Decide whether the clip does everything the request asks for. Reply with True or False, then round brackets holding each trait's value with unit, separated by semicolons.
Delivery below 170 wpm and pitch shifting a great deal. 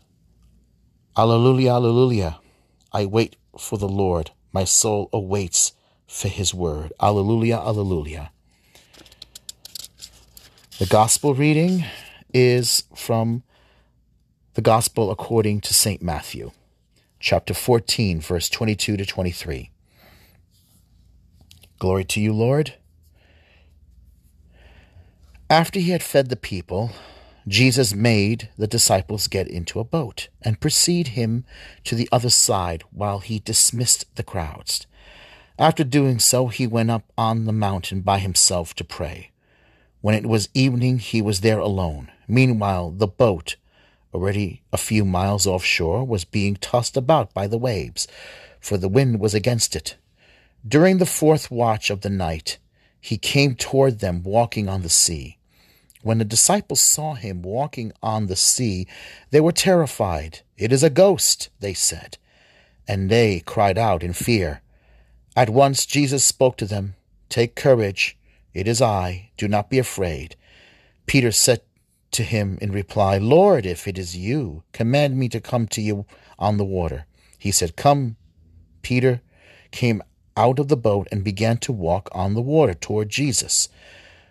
False (140 wpm; 4.9 semitones)